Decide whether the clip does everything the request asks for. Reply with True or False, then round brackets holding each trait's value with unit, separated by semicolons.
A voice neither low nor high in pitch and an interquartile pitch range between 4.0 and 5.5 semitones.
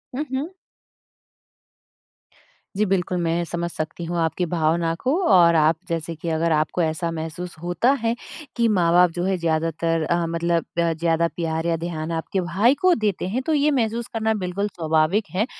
False (170 Hz; 3.2 semitones)